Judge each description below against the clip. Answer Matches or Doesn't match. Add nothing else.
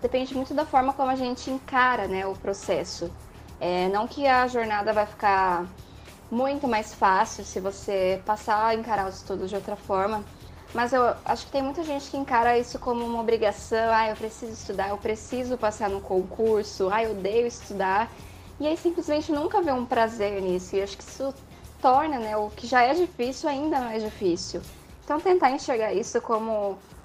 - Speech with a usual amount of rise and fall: Matches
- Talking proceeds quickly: Matches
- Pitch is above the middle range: Matches